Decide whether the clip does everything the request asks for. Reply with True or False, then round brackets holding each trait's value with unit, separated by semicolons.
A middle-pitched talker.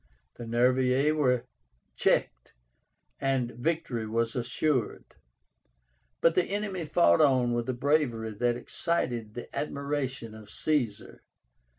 False (125 Hz)